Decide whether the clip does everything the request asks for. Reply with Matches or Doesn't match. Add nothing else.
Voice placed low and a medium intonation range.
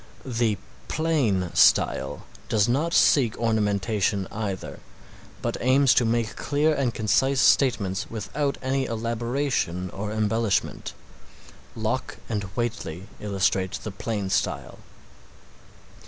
Matches